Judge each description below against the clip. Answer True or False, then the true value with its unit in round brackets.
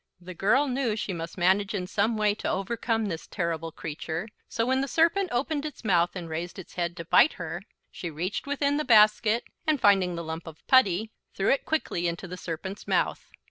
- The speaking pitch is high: True (200 Hz)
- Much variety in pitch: True (5.9 semitones)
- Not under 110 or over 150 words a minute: False (205 wpm)